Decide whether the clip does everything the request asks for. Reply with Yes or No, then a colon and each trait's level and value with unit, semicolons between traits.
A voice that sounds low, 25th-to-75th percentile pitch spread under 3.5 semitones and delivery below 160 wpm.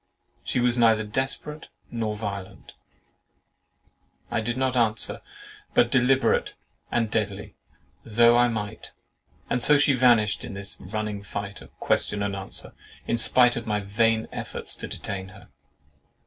Yes: low, 110 Hz; average, 2.8 semitones; slow, 135 wpm